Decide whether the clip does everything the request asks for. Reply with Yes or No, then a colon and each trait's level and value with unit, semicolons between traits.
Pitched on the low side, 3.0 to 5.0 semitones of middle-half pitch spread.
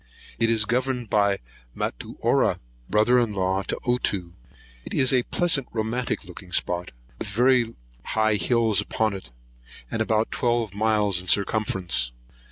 Yes: low, 110 Hz; average, 3.4 semitones